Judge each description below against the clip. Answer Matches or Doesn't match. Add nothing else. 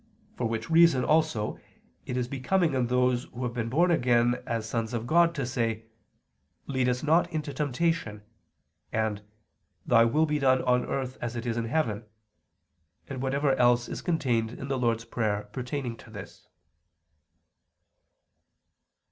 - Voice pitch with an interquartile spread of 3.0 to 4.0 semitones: Matches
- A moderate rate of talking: Matches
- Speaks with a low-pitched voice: Matches